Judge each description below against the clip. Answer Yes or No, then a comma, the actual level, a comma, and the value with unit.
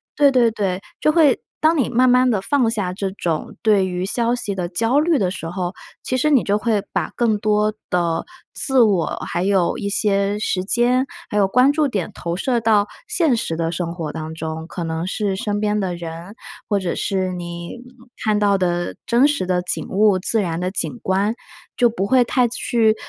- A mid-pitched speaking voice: No, high, 205 Hz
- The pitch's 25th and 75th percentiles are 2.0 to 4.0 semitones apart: No, average, 4.8 semitones